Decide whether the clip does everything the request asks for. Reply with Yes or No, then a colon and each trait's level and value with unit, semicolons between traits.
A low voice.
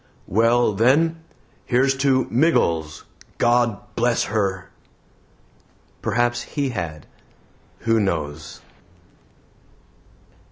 Yes: low, 115 Hz